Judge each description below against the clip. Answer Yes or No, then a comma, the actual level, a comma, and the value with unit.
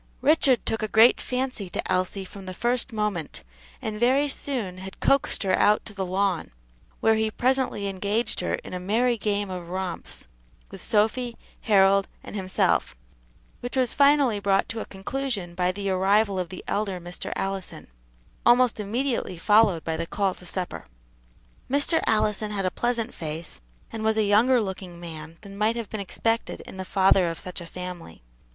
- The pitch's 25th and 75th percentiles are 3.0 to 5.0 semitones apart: Yes, average, 3.8 semitones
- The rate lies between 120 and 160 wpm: No, average, 175 wpm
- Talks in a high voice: Yes, high, 205 Hz